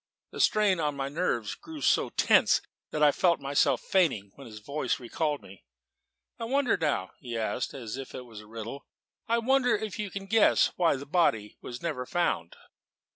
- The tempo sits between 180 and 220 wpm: Yes, average, 185 wpm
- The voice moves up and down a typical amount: No, wide, 8.5 semitones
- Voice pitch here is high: No, medium, 145 Hz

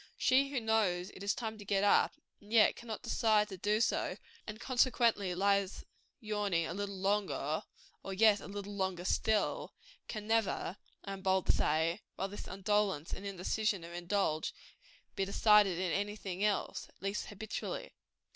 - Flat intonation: Yes, narrow, 2.1 semitones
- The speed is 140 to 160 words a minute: No, average, 170 wpm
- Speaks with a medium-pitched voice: No, high, 200 Hz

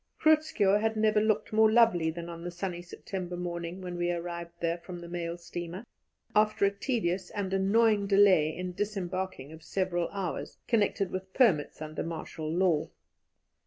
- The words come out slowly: No, average, 165 wpm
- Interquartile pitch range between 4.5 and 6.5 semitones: No, average, 3.1 semitones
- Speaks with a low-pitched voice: No, medium, 185 Hz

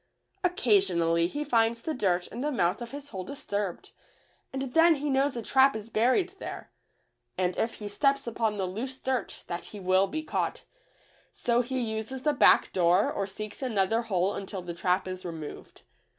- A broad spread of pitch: Yes, wide, 6.0 semitones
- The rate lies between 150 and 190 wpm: Yes, average, 180 wpm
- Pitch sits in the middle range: No, high, 220 Hz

